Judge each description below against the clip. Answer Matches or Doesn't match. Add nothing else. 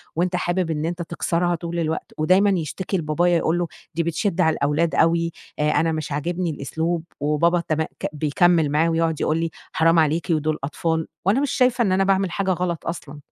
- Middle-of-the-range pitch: Matches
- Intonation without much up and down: Matches